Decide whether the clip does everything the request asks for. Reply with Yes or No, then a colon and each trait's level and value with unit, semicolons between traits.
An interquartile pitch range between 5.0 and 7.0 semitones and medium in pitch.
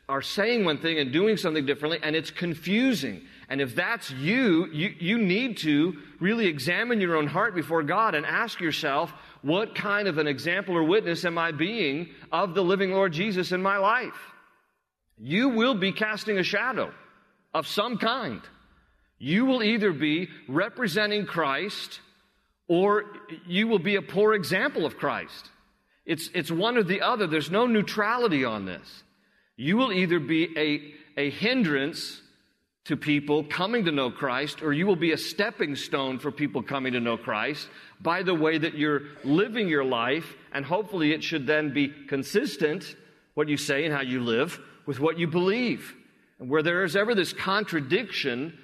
Yes: wide, 5.4 semitones; medium, 170 Hz